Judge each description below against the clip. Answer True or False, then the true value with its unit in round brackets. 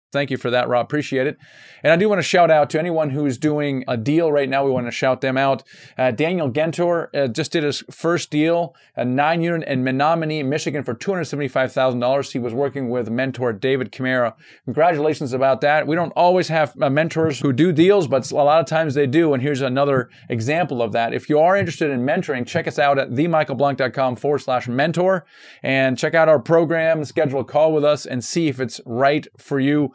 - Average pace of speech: False (215 wpm)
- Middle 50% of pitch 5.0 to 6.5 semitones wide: False (3.3 semitones)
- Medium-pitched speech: True (145 Hz)